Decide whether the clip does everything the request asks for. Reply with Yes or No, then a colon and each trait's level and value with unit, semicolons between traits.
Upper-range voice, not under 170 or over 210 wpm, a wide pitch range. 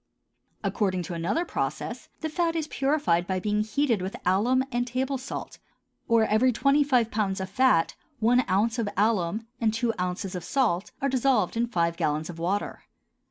Yes: high, 220 Hz; average, 175 wpm; wide, 5.7 semitones